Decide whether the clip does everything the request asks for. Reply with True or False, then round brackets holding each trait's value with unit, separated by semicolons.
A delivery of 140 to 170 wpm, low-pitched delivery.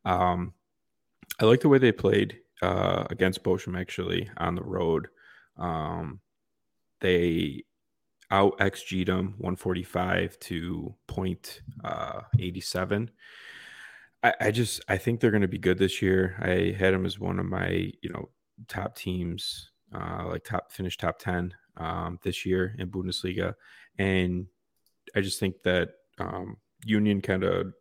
True (150 wpm; 95 Hz)